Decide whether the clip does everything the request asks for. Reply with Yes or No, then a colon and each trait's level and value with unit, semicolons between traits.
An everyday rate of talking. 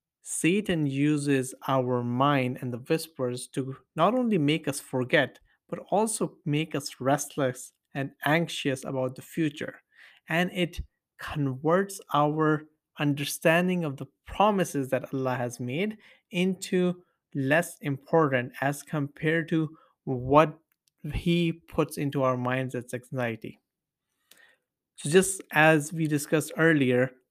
No: slow, 120 wpm